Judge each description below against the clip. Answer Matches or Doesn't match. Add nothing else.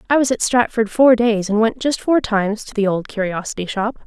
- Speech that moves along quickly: Matches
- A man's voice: Doesn't match